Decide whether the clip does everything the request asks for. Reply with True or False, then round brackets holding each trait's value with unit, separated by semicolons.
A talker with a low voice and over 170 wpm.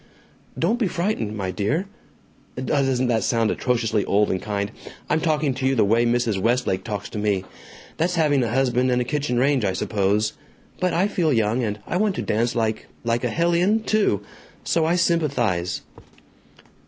True (125 Hz; 180 wpm)